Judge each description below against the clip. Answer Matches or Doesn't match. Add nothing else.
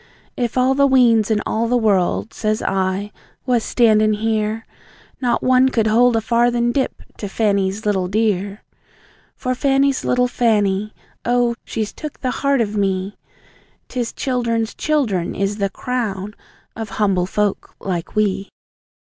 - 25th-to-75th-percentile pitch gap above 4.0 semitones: Doesn't match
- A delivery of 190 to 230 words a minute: Doesn't match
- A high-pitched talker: Matches